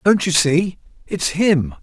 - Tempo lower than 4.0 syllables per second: Yes, 3.6 syllables/s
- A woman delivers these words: No, male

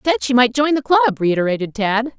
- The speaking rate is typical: No, fast, 245 wpm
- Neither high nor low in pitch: No, high, 245 Hz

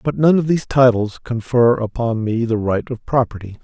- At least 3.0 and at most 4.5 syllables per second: No, 5.2 syllables/s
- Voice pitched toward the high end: No, low, 120 Hz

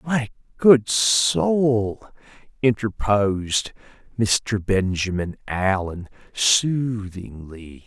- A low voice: Yes, low, 105 Hz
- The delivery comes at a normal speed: No, slow, 60 wpm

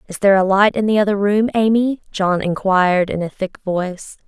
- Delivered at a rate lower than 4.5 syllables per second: No, 5.4 syllables/s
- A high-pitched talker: Yes, high, 200 Hz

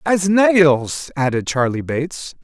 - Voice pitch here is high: No, medium, 155 Hz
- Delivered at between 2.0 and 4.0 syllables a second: Yes, 3.6 syllables/s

